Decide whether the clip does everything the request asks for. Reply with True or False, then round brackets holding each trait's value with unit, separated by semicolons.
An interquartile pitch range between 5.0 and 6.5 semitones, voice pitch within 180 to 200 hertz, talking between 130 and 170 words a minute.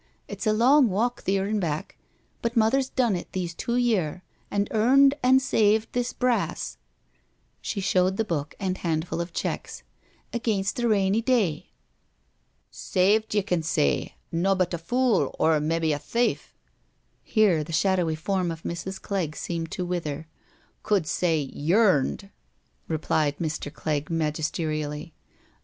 True (5.4 semitones; 185 Hz; 150 wpm)